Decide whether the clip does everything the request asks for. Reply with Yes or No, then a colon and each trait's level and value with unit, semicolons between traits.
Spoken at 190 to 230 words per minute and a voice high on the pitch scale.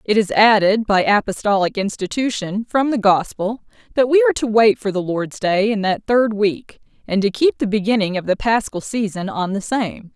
Yes: average, 200 wpm; high, 210 Hz